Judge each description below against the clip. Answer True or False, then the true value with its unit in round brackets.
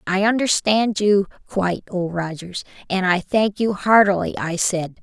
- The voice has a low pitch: False (195 Hz)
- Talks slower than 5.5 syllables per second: True (4.4 syllables/s)